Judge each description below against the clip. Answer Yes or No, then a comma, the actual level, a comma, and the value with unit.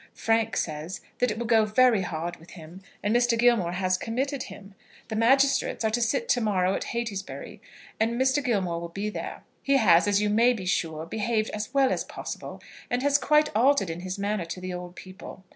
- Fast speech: Yes, fast, 210 wpm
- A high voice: Yes, high, 215 Hz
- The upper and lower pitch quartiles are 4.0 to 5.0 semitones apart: Yes, average, 4.7 semitones